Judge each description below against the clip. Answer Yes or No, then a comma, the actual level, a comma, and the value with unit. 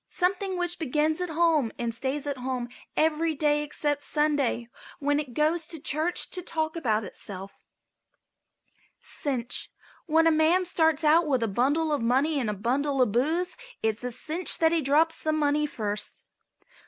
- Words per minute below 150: No, average, 165 wpm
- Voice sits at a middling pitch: No, very high, 300 Hz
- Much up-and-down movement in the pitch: No, average, 4.2 semitones